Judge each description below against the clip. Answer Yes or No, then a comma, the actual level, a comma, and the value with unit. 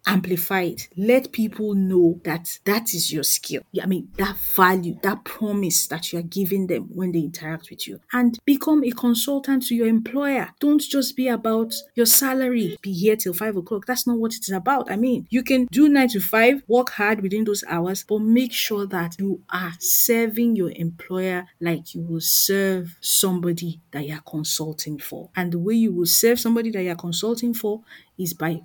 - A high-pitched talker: Yes, high, 200 Hz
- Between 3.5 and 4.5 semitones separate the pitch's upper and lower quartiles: No, average, 5.0 semitones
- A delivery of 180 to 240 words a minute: Yes, average, 200 wpm